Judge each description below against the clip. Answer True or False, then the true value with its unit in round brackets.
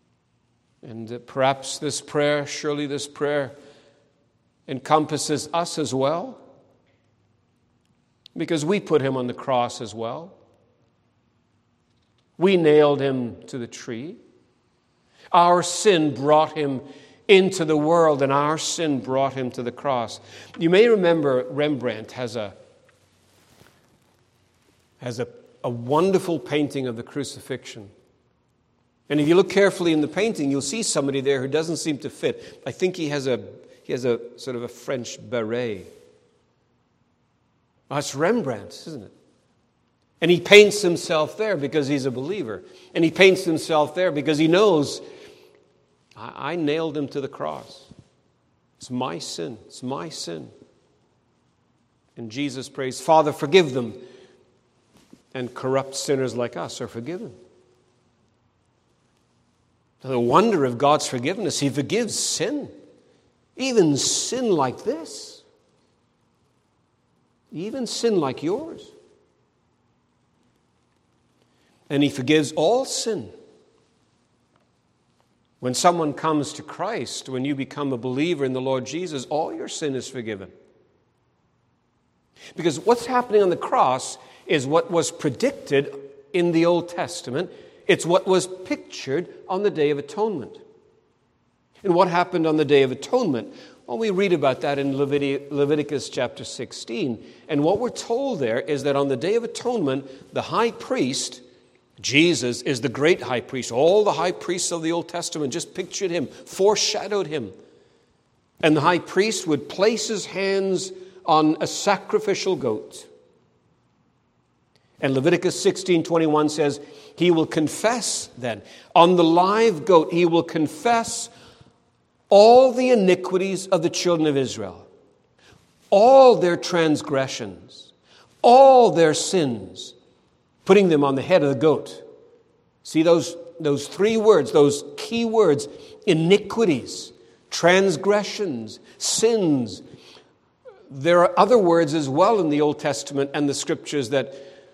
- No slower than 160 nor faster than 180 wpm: False (135 wpm)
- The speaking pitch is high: False (155 Hz)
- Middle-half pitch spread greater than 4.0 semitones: True (5.5 semitones)